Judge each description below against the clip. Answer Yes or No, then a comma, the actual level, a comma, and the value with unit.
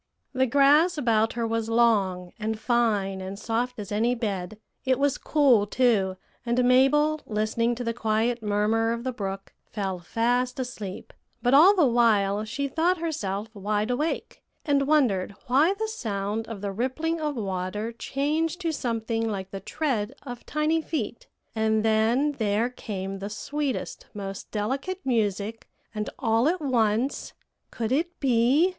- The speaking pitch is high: Yes, high, 230 Hz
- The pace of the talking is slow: No, average, 155 wpm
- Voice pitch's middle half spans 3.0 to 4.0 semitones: No, average, 4.6 semitones